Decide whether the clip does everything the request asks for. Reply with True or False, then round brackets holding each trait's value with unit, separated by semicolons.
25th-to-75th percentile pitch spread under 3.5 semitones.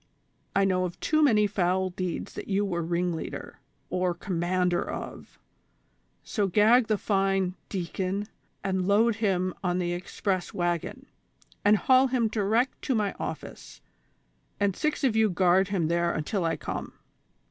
True (2.9 semitones)